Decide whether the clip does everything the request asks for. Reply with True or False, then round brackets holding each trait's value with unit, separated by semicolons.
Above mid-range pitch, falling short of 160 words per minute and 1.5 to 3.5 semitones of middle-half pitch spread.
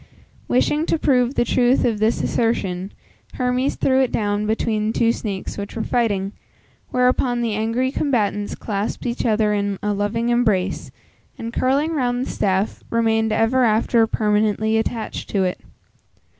True (225 Hz; 150 wpm; 2.9 semitones)